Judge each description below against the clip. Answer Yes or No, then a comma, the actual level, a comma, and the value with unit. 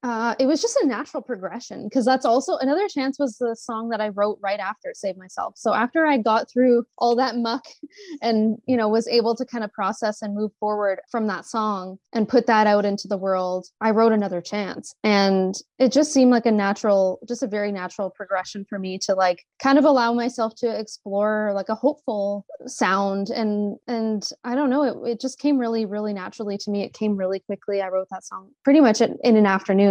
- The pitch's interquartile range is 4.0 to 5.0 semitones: No, average, 3.6 semitones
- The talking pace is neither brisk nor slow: No, fast, 220 wpm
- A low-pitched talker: No, high, 220 Hz